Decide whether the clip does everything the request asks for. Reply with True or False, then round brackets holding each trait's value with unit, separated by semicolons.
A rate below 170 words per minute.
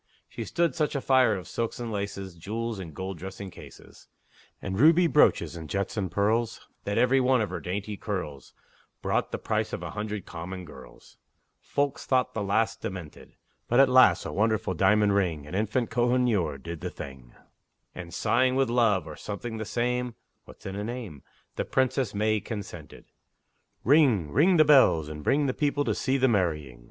False (185 wpm)